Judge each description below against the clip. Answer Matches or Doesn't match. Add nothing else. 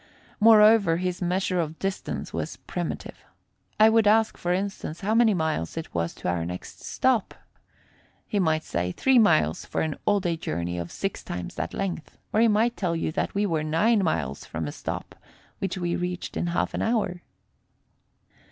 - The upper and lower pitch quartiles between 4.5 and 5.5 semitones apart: Matches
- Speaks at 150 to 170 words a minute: Doesn't match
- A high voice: Doesn't match